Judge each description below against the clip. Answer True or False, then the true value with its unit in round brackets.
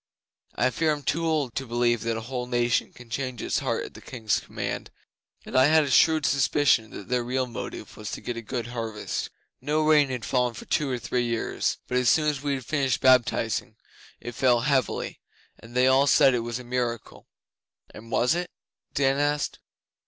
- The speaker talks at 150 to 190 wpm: False (205 wpm)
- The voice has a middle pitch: False (125 Hz)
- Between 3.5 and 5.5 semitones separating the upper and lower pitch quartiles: False (2.9 semitones)